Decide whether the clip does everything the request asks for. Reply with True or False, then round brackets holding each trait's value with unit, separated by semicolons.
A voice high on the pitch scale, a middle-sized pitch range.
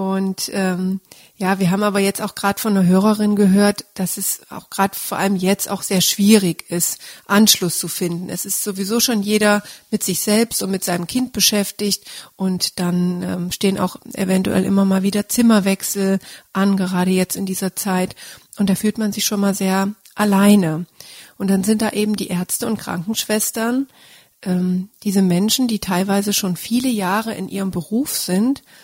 False (195 Hz; 2.0 semitones)